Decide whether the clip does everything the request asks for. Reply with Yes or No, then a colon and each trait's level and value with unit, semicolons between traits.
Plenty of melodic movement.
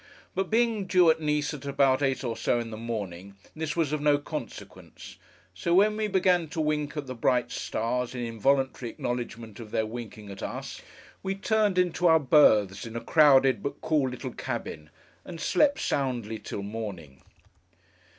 Yes: wide, 6.0 semitones